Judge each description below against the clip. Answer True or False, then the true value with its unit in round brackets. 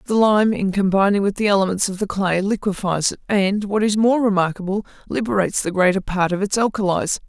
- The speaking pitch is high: True (200 Hz)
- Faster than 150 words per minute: True (200 wpm)